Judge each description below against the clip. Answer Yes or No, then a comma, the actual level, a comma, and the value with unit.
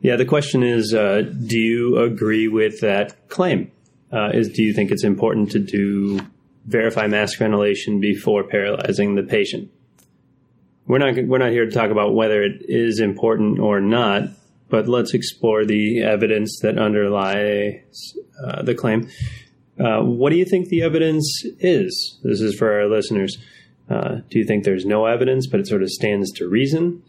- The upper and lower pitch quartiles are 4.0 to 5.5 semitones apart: No, average, 2.9 semitones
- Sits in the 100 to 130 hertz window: Yes, low, 110 Hz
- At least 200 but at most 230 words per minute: No, average, 175 wpm